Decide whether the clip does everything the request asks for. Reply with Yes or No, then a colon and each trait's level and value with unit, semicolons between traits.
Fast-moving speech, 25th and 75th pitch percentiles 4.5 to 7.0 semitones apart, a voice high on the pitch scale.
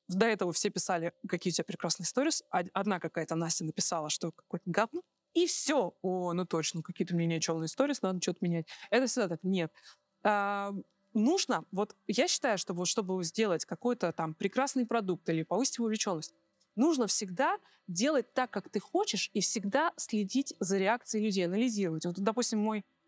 Yes: fast, 170 wpm; average, 4.8 semitones; high, 200 Hz